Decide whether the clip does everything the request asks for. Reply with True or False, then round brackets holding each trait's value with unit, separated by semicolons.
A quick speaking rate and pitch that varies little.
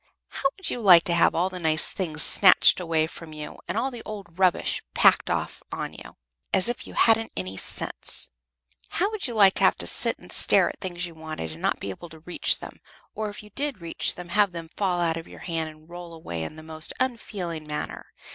False (235 wpm; 4.4 semitones)